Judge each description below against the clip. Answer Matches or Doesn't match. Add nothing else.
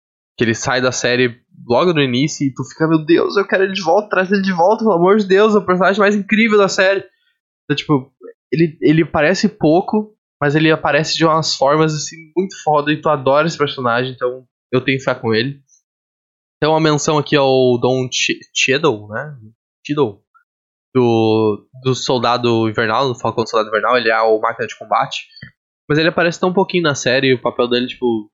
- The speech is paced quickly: Matches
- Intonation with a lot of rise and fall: Matches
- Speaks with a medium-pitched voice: Matches